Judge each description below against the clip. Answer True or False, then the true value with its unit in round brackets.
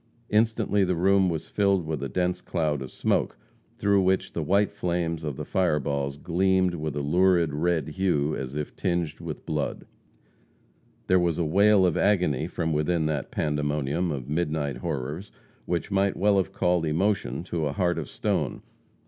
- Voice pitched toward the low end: True (85 Hz)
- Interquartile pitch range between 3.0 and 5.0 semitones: True (3.8 semitones)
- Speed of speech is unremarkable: True (170 wpm)